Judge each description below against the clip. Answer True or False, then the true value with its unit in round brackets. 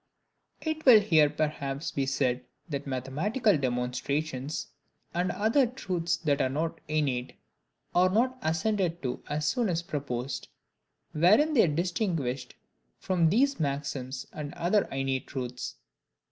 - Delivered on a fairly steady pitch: False (5.5 semitones)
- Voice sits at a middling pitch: True (155 Hz)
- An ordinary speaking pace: False (130 wpm)